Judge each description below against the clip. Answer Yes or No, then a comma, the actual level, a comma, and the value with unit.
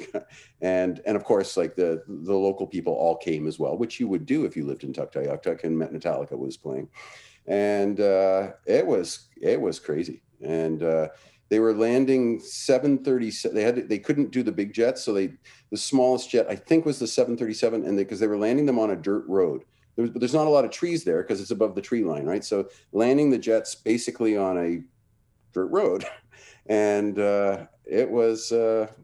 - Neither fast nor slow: No, fast, 210 wpm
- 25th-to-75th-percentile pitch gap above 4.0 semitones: Yes, average, 4.4 semitones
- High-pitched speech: No, low, 110 Hz